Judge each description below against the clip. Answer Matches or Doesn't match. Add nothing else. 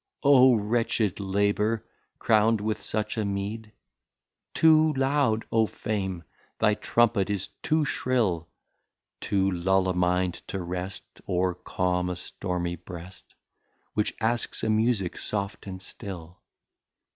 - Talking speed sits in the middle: Doesn't match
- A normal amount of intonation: Matches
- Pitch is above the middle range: Doesn't match